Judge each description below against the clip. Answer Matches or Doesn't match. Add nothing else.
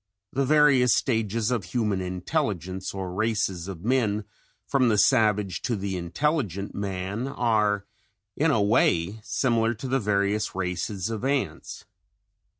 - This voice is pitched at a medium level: Doesn't match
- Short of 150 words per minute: Matches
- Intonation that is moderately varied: Matches